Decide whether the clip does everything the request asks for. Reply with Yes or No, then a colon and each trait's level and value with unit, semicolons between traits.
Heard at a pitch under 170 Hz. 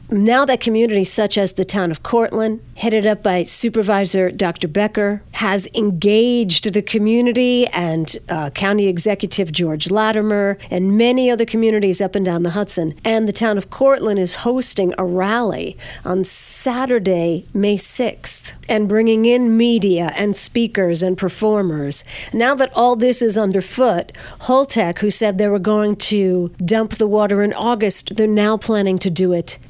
No: high, 205 Hz